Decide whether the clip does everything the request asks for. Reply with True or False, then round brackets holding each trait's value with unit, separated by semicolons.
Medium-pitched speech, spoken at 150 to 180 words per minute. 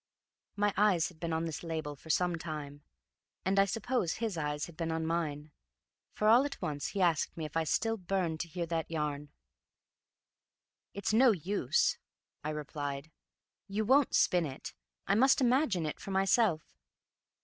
True (170 Hz; 170 wpm)